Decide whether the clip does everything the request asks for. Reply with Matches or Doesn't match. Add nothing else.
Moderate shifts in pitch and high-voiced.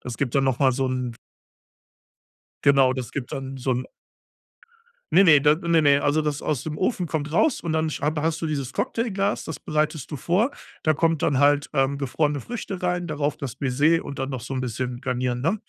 Doesn't match